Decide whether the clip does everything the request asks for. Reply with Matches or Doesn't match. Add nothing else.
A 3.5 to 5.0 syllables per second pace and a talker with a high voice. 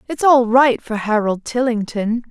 Matches